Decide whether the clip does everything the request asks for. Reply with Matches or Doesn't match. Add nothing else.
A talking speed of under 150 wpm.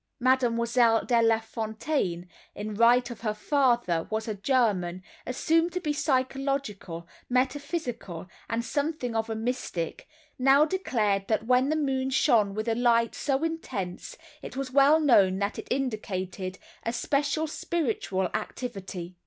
Matches